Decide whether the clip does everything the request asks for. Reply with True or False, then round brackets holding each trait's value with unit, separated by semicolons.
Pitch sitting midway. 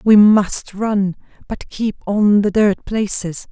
False (205 Hz)